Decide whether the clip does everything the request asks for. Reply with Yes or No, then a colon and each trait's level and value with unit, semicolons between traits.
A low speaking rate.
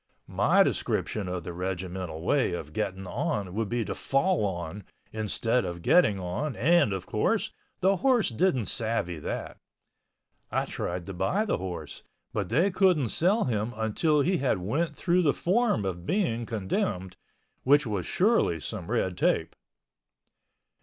No: average, 155 wpm